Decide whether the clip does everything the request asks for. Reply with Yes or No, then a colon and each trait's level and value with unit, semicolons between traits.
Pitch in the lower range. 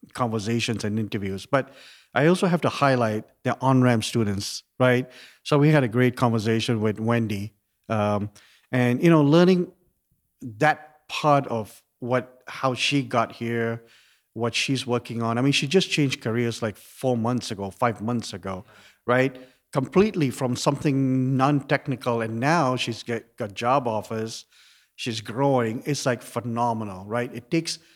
Yes: low, 120 Hz